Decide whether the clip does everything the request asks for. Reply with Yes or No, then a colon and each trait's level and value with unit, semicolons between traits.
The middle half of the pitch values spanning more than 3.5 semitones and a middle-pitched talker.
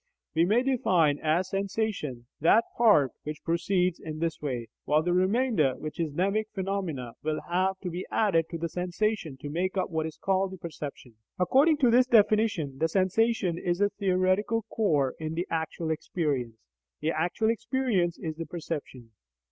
Yes: average, 4.4 semitones; medium, 175 Hz